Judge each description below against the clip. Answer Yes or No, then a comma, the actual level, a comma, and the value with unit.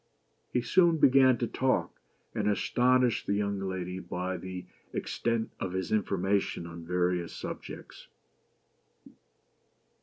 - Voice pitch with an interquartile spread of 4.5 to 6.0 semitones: Yes, average, 4.9 semitones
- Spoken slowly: Yes, slow, 115 wpm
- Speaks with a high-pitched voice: No, low, 100 Hz